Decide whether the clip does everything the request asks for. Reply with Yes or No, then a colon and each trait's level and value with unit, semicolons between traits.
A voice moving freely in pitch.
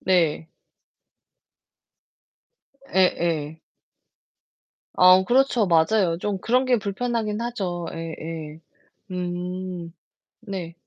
No: average, 4.1 semitones